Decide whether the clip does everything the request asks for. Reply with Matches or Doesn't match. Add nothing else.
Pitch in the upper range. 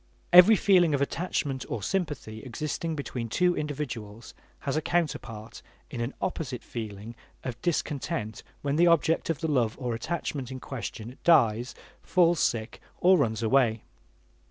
Doesn't match